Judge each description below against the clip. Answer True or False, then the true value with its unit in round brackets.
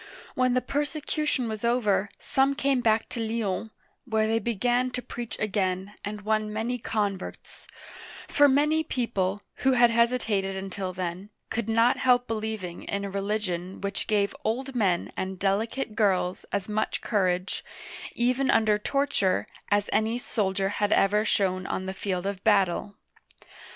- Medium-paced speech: True (150 wpm)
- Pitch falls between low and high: False (215 Hz)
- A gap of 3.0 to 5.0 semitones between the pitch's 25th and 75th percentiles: True (3.7 semitones)